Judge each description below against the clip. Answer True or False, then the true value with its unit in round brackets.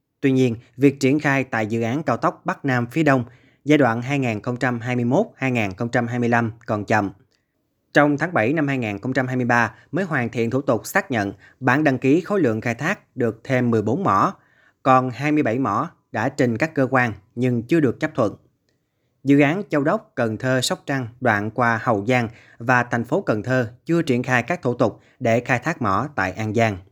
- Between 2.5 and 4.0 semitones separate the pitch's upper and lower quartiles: True (3.4 semitones)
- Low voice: True (125 Hz)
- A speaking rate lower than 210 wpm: True (190 wpm)